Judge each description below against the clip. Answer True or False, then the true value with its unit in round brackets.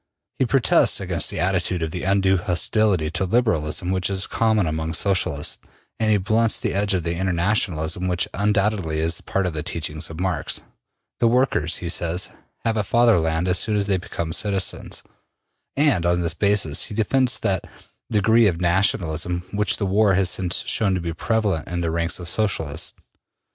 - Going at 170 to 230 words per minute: True (175 wpm)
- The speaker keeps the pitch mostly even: False (3.7 semitones)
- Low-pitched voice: True (95 Hz)